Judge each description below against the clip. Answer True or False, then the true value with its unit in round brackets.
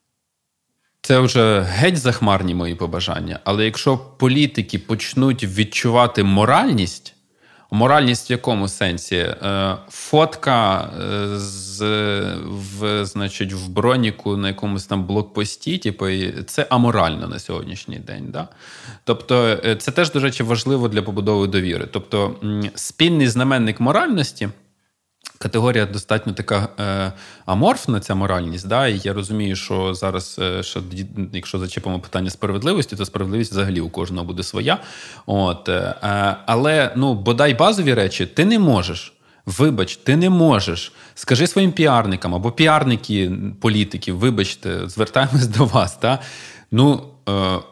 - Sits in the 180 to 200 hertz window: False (105 Hz)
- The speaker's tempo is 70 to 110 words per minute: False (120 wpm)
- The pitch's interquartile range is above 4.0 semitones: True (4.5 semitones)